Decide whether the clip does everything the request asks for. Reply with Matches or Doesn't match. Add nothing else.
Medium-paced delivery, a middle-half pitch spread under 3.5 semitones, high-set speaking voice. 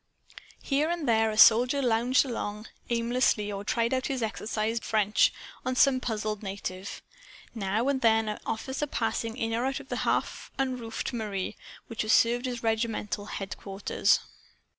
Matches